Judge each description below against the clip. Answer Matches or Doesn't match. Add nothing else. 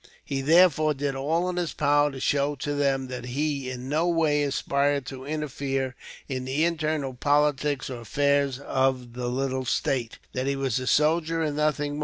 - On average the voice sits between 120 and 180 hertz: Matches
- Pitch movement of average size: Doesn't match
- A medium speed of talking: Matches